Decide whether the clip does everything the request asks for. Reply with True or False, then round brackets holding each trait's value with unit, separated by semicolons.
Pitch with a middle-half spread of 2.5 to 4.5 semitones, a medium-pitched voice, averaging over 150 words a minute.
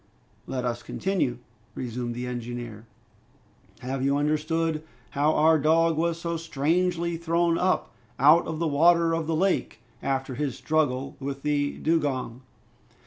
False (4.0 semitones; 150 Hz; 140 wpm)